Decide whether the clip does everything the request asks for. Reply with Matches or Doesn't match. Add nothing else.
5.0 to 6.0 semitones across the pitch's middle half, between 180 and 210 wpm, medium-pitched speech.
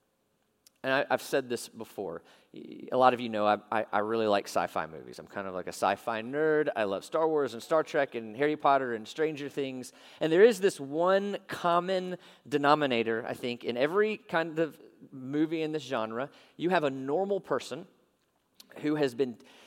Matches